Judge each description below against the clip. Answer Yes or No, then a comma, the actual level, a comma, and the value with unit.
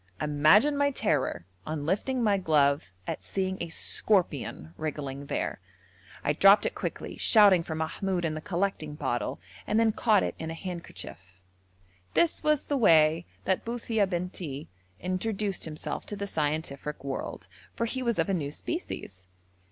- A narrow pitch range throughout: No, wide, 5.6 semitones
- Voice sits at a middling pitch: Yes, medium, 175 Hz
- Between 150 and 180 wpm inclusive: Yes, average, 155 wpm